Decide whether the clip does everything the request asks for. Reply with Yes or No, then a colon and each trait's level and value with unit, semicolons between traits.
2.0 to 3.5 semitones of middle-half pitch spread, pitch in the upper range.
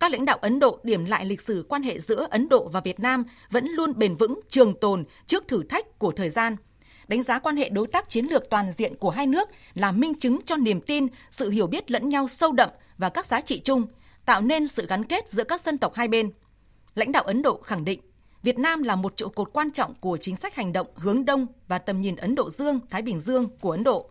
No: average, 5.2 semitones; high, 235 Hz